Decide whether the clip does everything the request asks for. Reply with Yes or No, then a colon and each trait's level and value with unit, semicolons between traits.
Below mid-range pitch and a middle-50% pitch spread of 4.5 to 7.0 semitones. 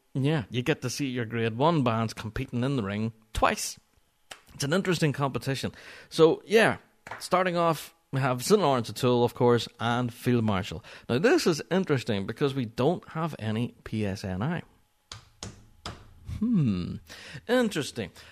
Yes: low, 125 Hz; wide, 5.5 semitones